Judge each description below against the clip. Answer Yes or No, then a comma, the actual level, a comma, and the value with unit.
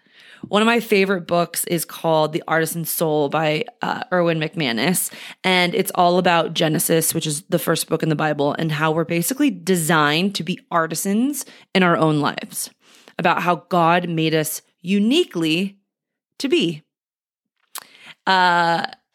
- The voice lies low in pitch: No, medium, 170 Hz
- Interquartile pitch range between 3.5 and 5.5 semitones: No, average, 2.8 semitones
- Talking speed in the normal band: Yes, average, 150 wpm